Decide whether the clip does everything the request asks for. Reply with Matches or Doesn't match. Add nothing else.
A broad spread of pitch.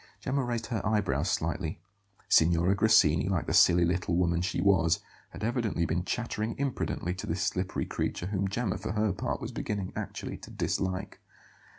Doesn't match